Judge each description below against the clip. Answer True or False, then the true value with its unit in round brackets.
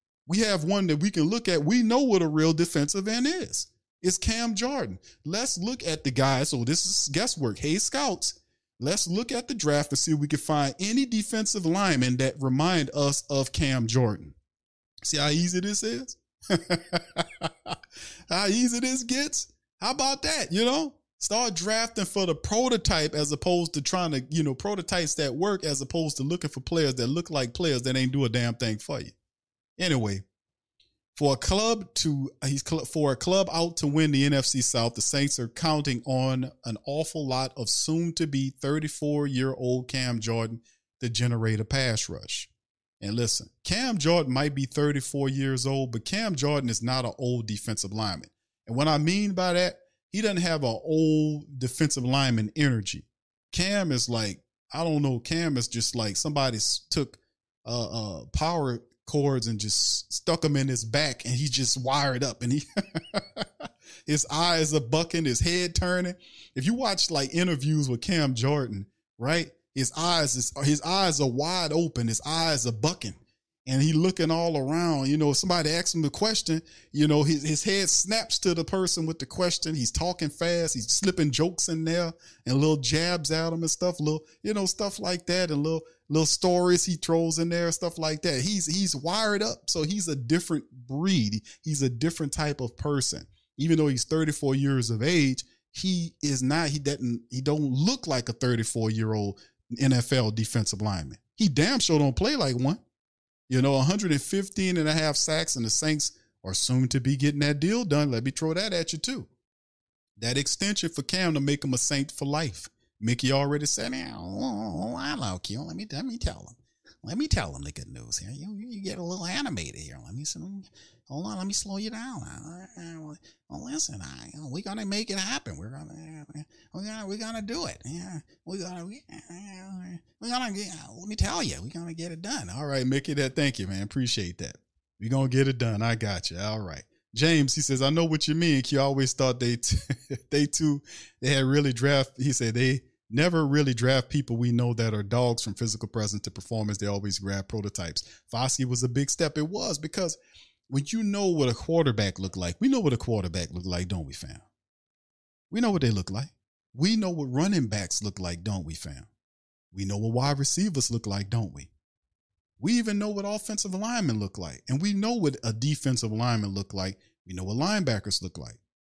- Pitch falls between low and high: True (145 Hz)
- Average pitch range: False (5.9 semitones)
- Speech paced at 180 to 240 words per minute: True (200 wpm)